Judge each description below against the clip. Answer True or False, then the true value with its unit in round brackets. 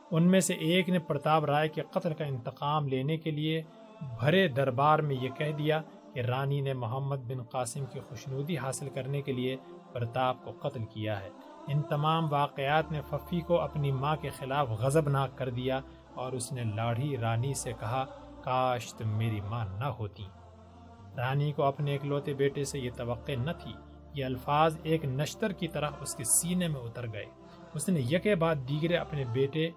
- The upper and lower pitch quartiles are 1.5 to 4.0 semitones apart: True (3.6 semitones)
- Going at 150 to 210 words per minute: True (190 wpm)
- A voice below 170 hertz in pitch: True (140 Hz)